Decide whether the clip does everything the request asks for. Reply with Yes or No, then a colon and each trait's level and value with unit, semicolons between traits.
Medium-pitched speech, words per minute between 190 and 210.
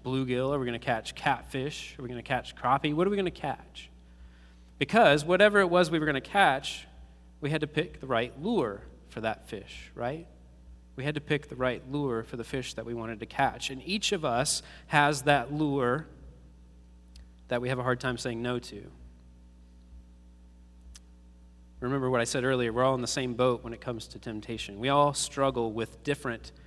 No: low, 120 Hz; fast, 205 wpm